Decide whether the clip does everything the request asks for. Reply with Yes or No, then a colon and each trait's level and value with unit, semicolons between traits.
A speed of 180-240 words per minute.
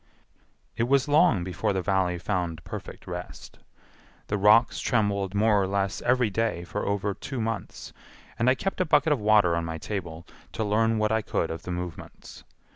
Yes: average, 185 wpm